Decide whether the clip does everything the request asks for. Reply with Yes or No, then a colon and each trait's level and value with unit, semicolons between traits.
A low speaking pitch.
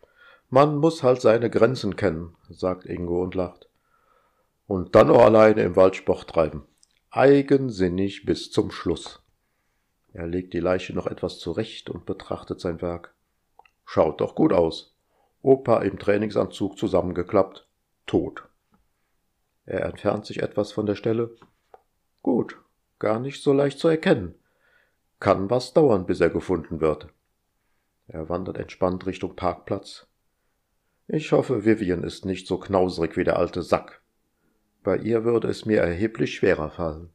Yes: very low, 95 Hz